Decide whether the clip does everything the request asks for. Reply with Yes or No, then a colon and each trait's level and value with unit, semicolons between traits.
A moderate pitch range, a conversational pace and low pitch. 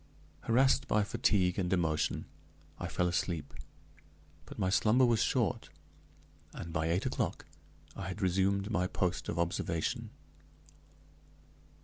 No: average, 3.7 semitones; slow, 120 wpm; very low, 95 Hz